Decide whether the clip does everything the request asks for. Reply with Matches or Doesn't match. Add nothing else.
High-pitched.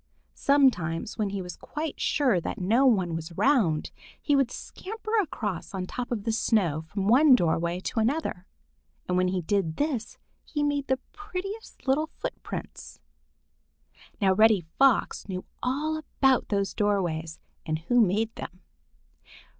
Matches